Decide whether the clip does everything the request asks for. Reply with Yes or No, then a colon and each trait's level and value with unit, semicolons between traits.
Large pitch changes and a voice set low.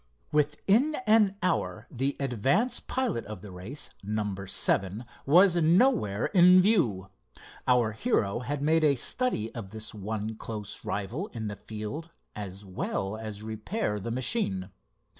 Yes: wide, 8.8 semitones; low, 115 Hz